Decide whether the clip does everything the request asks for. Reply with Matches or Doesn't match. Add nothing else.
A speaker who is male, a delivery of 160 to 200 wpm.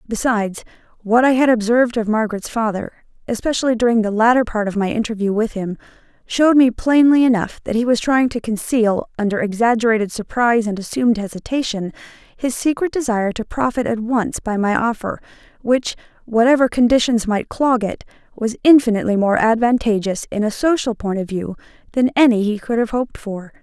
Doesn't match